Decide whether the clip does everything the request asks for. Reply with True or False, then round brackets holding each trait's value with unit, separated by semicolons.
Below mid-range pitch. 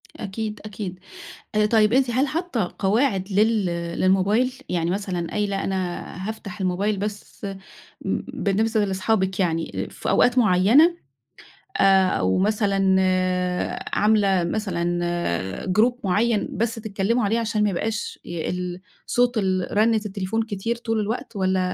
False (205 Hz)